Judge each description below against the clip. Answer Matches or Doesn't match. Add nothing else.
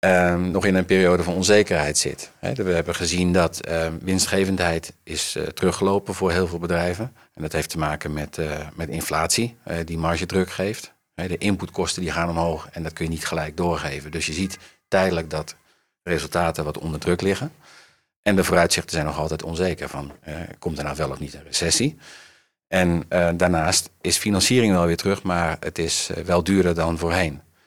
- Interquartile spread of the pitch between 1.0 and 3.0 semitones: Matches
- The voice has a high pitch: Doesn't match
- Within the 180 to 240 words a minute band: Matches